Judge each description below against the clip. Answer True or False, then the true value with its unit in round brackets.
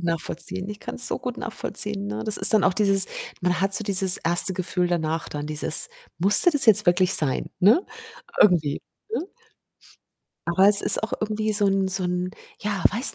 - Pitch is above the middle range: True (195 Hz)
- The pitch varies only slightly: False (3.0 semitones)